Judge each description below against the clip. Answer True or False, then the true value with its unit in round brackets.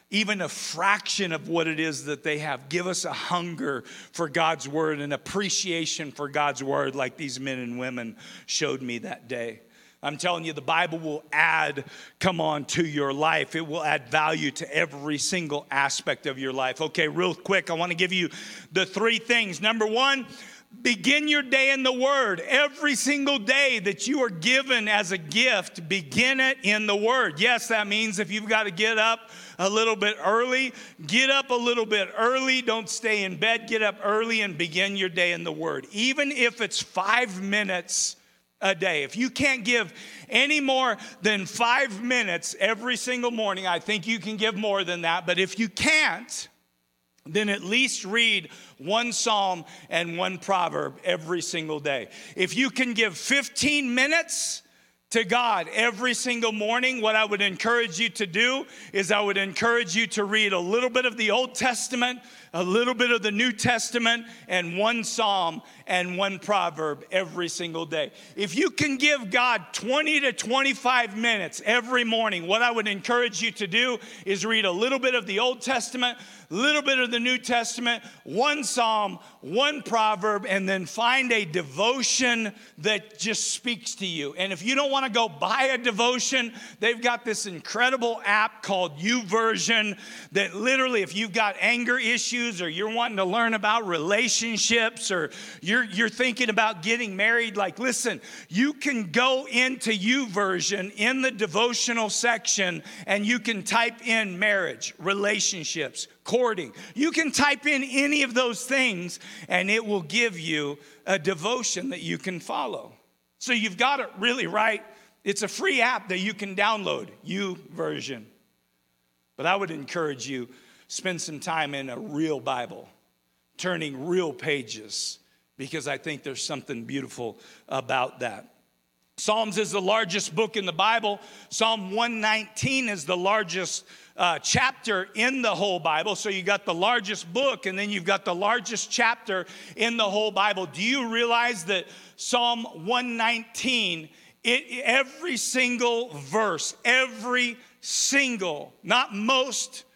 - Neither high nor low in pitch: False (215 Hz)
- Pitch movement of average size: True (4.9 semitones)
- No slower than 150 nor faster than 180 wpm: True (170 wpm)